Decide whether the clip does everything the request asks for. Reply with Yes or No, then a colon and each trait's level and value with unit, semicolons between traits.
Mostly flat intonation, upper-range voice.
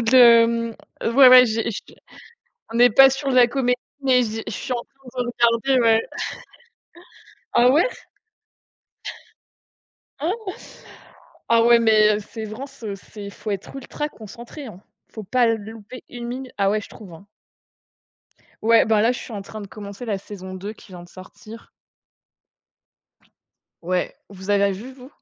No: average, 3.3 semitones; high, 230 Hz